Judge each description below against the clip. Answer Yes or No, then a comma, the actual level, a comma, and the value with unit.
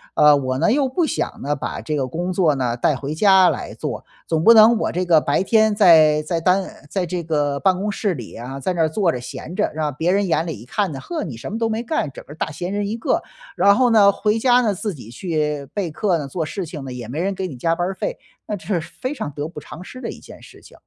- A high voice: No, medium, 175 Hz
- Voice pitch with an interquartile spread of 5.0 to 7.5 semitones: Yes, wide, 5.5 semitones